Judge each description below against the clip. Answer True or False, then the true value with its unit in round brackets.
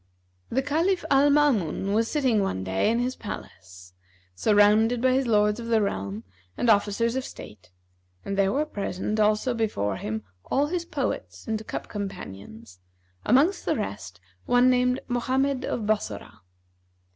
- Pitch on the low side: False (220 Hz)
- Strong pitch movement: True (5.9 semitones)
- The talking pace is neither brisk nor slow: True (150 wpm)